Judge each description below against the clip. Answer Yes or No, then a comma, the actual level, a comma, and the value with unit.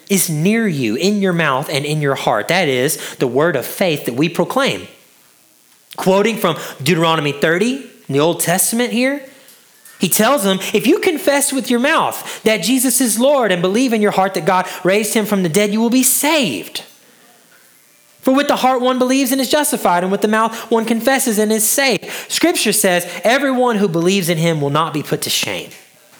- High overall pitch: Yes, high, 215 Hz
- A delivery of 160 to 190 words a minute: No, average, 200 wpm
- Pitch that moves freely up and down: Yes, wide, 6.1 semitones